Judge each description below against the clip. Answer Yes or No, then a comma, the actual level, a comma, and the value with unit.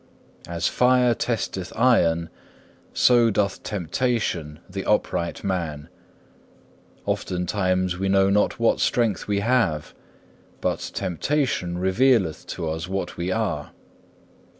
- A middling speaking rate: No, slow, 105 wpm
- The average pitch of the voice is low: Yes, very low, 95 Hz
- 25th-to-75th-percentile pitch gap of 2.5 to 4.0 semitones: No, average, 5.2 semitones